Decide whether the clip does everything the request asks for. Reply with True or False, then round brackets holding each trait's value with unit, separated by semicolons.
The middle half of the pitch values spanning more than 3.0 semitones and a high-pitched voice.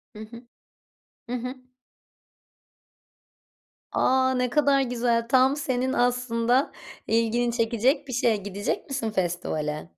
False (2.4 semitones; 240 Hz)